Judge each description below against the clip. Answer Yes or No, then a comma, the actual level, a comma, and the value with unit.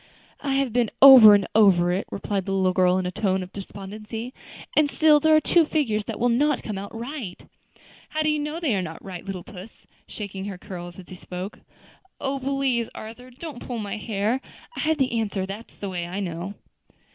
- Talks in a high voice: Yes, high, 215 Hz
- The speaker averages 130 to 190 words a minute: No, fast, 205 wpm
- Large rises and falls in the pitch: Yes, wide, 5.8 semitones